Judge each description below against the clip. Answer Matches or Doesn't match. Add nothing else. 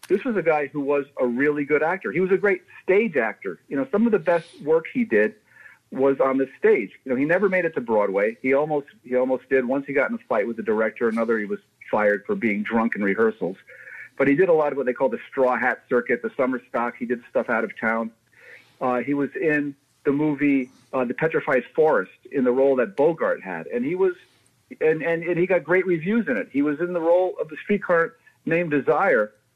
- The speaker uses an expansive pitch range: Matches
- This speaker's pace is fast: Matches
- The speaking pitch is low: Doesn't match